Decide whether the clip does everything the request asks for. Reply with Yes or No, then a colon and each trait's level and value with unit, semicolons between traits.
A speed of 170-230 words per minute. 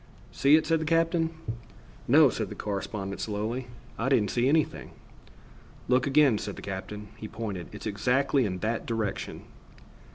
No: average, 155 wpm